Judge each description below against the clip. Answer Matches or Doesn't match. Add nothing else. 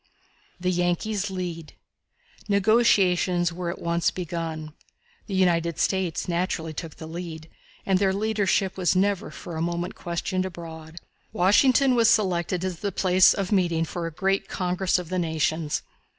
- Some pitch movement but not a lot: Doesn't match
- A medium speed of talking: Matches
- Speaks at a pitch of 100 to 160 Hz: Doesn't match